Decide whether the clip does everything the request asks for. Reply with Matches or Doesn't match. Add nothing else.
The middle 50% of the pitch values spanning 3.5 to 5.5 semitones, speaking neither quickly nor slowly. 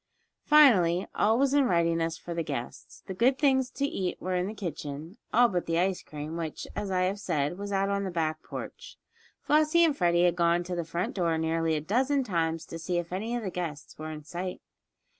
Doesn't match